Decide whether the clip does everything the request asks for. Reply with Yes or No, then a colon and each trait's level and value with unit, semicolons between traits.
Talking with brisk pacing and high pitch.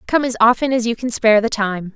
Yes: fast, 275 wpm; high, 230 Hz